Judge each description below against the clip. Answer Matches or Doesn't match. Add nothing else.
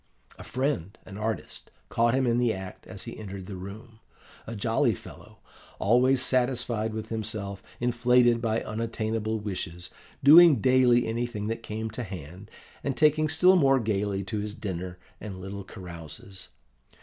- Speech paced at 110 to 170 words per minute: Matches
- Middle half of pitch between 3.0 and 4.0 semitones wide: Matches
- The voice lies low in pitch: Matches